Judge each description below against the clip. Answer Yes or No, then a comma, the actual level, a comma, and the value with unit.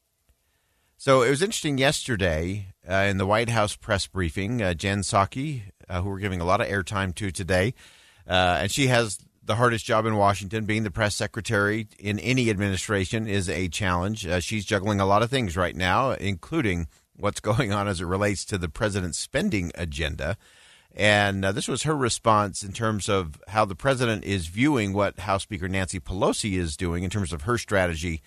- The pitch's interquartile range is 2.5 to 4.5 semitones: Yes, average, 3.0 semitones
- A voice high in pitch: No, low, 100 Hz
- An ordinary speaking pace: Yes, average, 195 wpm